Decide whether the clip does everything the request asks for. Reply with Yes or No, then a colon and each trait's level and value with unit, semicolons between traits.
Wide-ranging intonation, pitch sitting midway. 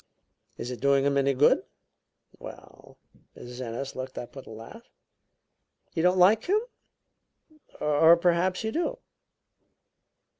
Yes: wide, 6.0 semitones; medium, 145 Hz